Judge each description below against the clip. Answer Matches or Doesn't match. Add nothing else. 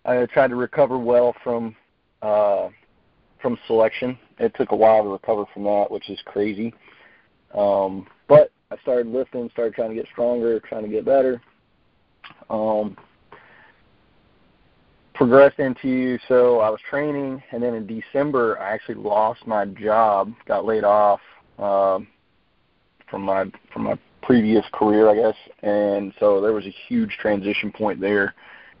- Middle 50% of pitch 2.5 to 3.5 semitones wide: Matches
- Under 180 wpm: Matches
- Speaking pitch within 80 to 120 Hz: Matches